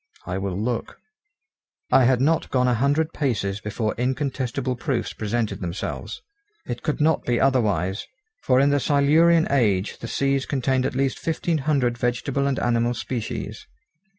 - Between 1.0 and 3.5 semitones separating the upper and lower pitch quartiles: Yes, average, 3.2 semitones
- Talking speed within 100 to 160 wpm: Yes, average, 150 wpm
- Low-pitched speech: Yes, low, 125 Hz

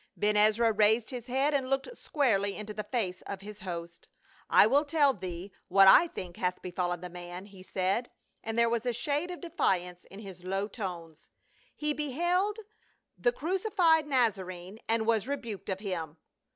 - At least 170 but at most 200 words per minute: Yes, average, 190 wpm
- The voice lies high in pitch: Yes, high, 215 Hz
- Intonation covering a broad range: Yes, wide, 6.6 semitones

